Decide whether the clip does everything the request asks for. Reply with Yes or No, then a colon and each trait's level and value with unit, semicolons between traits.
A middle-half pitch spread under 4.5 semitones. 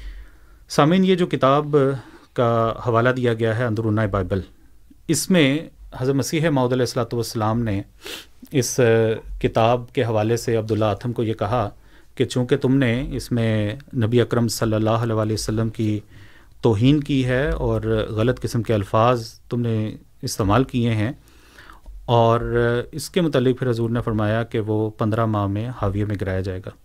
Yes: average, 2.8 semitones